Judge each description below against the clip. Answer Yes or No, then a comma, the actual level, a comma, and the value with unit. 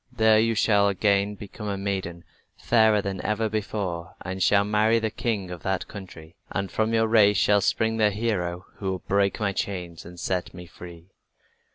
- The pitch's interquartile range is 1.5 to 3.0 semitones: Yes, average, 2.7 semitones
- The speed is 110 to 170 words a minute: No, average, 185 wpm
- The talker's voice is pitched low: Yes, low, 100 Hz